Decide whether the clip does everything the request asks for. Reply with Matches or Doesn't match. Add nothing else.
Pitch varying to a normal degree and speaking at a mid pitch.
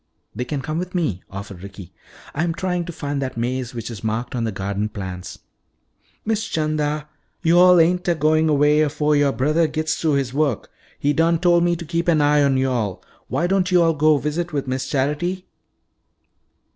Matches